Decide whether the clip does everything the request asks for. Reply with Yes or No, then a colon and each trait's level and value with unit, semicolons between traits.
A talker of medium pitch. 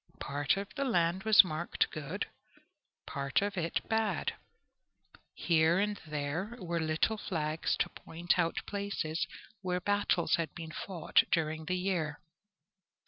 Yes: medium, 170 Hz